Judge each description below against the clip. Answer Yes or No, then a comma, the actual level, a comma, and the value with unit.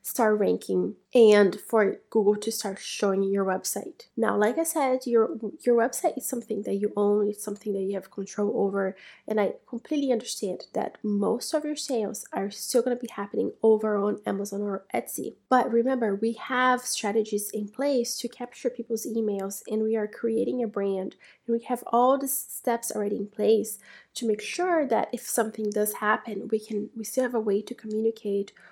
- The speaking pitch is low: No, high, 220 Hz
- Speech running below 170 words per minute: No, average, 190 wpm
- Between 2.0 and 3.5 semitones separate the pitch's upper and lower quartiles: Yes, average, 2.7 semitones